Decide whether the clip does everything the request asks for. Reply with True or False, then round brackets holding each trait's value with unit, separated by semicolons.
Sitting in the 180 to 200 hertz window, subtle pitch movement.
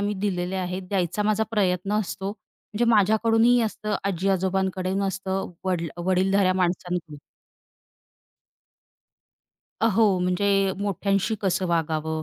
True (190 Hz; 2.2 semitones)